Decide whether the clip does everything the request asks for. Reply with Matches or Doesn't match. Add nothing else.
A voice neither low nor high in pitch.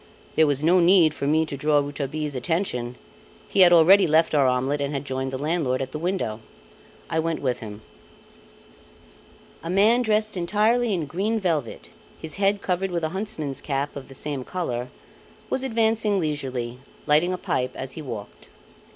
Matches